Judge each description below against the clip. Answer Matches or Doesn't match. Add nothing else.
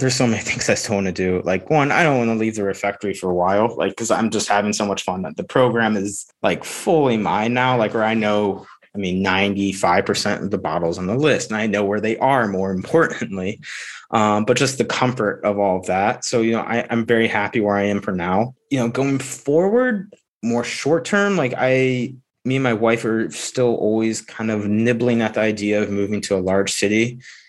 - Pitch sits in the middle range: Doesn't match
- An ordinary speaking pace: Doesn't match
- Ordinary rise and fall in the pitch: Matches